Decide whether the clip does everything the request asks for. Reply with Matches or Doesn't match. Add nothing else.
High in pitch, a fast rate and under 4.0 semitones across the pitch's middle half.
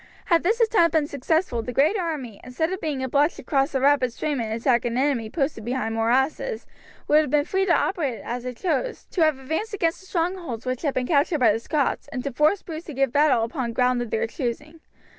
Doesn't match